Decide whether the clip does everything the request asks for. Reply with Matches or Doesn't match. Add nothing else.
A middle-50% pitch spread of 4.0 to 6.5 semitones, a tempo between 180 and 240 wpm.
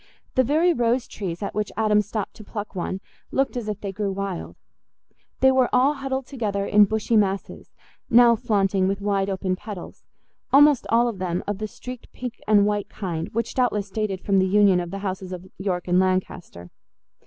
Doesn't match